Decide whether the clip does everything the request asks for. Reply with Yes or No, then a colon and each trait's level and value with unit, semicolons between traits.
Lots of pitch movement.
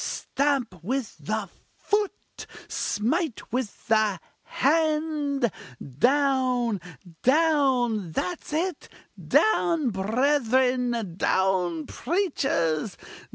Yes: wide, 5.7 semitones